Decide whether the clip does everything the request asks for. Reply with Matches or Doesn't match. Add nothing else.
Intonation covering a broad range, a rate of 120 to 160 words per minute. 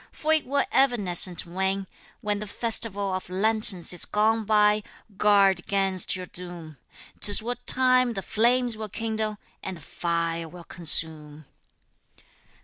Doesn't match